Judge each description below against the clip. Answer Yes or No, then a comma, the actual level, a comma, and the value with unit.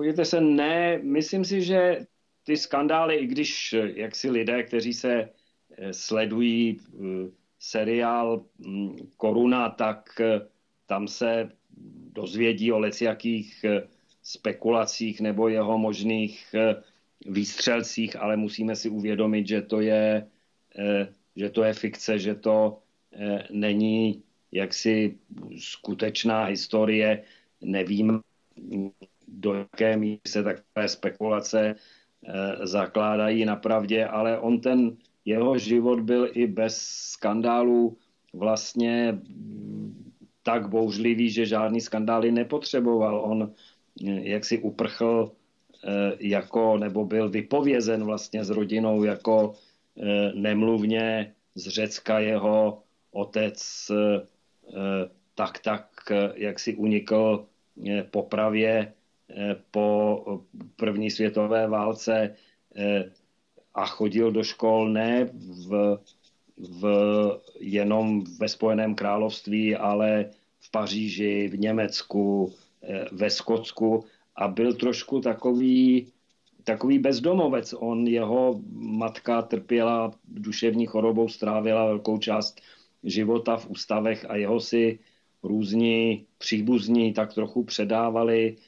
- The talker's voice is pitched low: Yes, low, 110 Hz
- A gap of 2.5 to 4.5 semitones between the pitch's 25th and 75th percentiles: No, narrow, 1.5 semitones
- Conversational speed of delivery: No, slow, 100 wpm